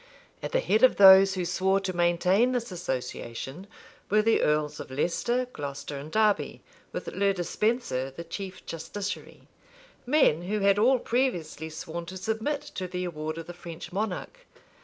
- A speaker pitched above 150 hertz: Yes, medium, 185 Hz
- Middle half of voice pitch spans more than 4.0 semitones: Yes, average, 4.8 semitones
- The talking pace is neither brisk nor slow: Yes, average, 160 wpm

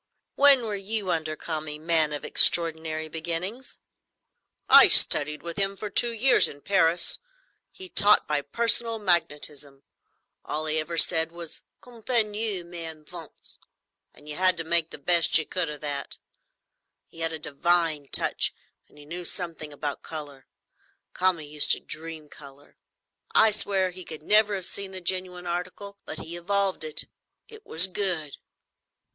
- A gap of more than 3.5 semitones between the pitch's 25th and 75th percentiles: Yes, average, 4.0 semitones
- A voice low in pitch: No, medium, 170 Hz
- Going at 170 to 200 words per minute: No, average, 155 wpm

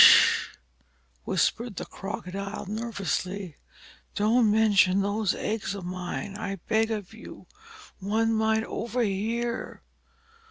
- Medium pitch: No, high, 210 Hz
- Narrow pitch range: Yes, narrow, 2.2 semitones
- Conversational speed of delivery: No, slow, 110 wpm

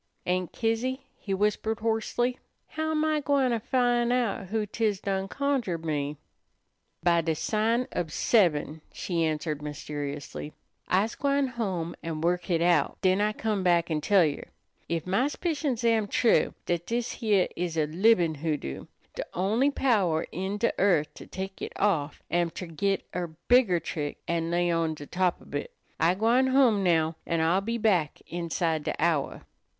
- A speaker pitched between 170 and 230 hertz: Yes, medium, 185 Hz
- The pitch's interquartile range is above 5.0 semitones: Yes, wide, 5.6 semitones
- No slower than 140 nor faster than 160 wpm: No, average, 175 wpm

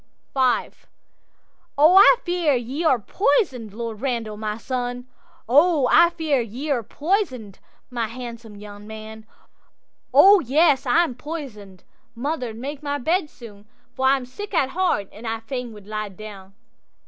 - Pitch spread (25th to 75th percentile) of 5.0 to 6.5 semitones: Yes, wide, 5.4 semitones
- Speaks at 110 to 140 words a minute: Yes, slow, 135 wpm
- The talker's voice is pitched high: Yes, very high, 250 Hz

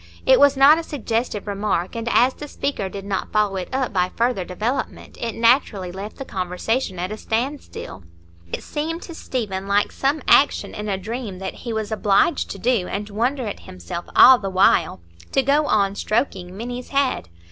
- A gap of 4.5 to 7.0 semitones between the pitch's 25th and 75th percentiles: Yes, average, 5.2 semitones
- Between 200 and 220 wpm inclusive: No, average, 185 wpm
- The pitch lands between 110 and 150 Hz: No, high, 215 Hz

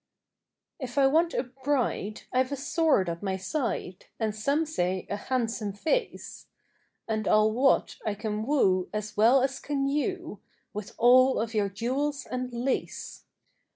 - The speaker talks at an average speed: Yes, average, 155 wpm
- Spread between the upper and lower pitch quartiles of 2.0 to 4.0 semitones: No, average, 4.7 semitones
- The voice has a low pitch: No, high, 245 Hz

